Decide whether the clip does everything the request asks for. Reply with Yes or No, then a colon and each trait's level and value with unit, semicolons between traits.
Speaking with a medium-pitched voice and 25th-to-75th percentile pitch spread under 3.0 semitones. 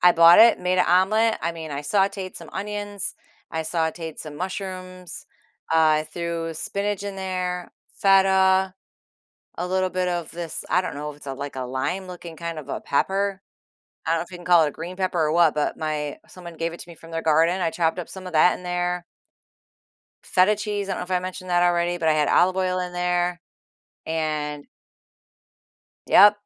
Yes: medium, 180 Hz; narrow, 2.4 semitones